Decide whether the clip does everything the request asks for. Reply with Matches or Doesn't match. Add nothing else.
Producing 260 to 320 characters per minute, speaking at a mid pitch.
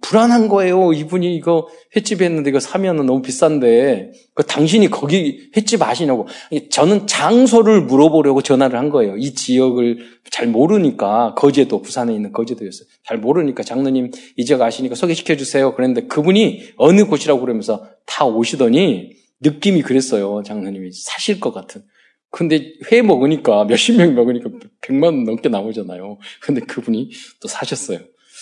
Doesn't match